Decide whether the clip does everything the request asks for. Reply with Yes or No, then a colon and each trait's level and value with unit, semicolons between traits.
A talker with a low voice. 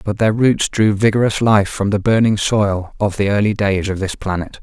Yes: low, 105 Hz